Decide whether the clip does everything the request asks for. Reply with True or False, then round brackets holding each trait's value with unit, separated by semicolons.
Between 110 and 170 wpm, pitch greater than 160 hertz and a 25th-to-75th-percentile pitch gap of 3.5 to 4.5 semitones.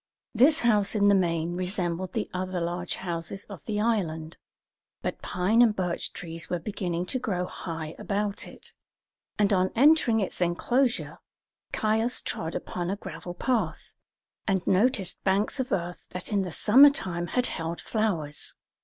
True (155 wpm; 190 Hz; 4.0 semitones)